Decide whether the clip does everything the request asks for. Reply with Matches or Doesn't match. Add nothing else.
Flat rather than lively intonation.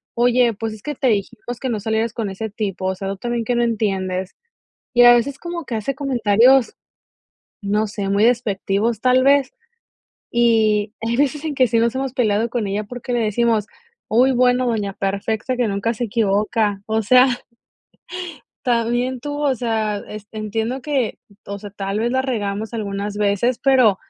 Doesn't match